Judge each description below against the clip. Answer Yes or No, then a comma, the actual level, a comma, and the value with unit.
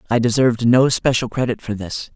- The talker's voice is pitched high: No, low, 120 Hz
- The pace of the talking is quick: No, average, 195 wpm